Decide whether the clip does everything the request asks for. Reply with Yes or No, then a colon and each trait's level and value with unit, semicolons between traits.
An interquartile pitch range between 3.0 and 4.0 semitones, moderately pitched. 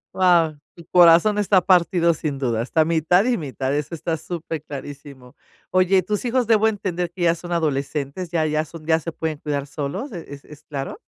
Yes: average, 3.6 semitones; medium, 165 Hz